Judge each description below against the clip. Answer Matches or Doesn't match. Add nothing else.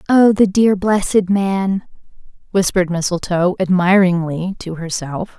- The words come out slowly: Matches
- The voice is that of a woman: Matches